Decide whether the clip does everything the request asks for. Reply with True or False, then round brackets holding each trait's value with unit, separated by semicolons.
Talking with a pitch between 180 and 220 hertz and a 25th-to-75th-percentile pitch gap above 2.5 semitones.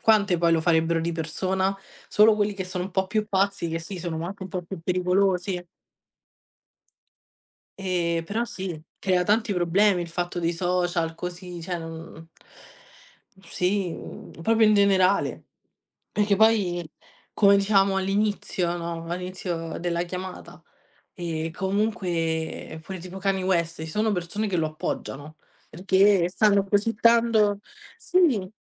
True (185 Hz; 2.9 semitones)